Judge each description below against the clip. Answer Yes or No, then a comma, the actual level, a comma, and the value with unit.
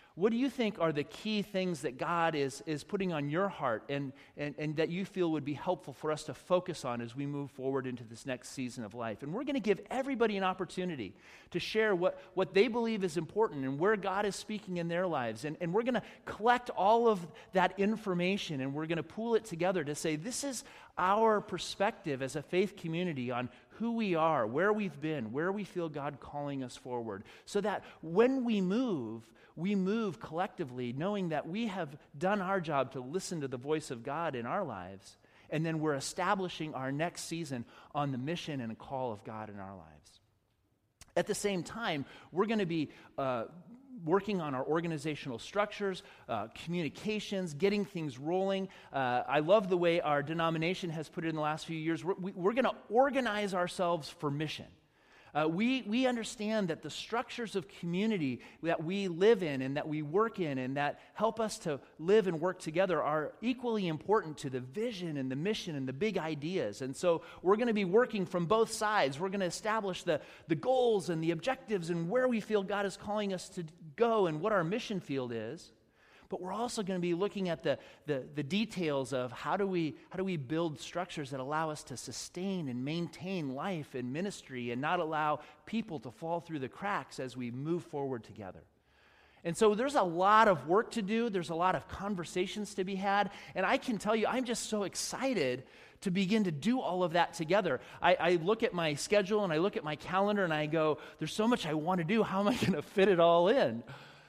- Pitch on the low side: No, medium, 175 Hz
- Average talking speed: No, fast, 215 wpm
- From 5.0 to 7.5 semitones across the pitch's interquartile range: Yes, wide, 5.5 semitones